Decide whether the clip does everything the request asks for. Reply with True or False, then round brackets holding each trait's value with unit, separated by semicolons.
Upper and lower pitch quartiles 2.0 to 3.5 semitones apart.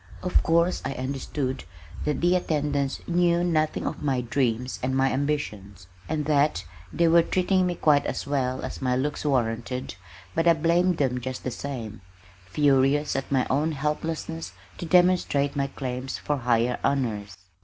False (4.0 semitones)